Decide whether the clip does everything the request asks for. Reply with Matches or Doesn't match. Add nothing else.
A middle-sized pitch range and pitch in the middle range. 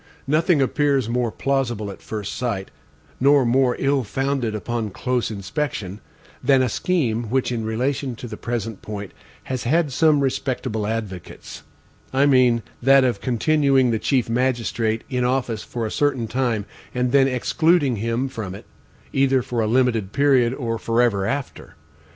Doesn't match